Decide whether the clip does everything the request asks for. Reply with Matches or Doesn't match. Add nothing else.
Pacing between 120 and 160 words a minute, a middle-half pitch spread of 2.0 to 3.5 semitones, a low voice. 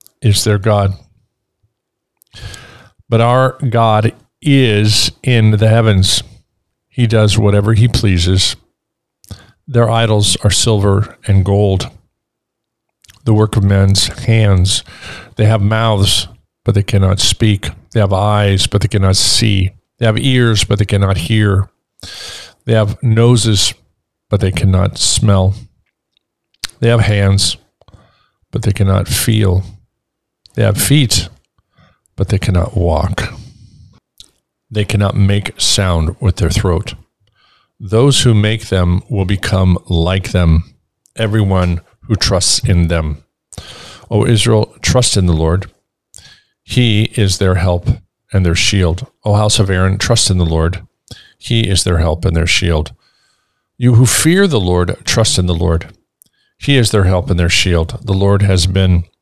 Matches